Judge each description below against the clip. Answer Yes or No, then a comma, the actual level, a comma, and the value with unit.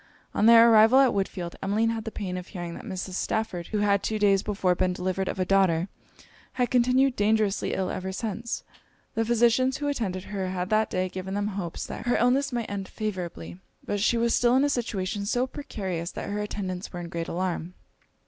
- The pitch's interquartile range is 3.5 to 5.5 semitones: Yes, average, 3.8 semitones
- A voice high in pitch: Yes, high, 200 Hz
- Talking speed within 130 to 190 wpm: No, fast, 205 wpm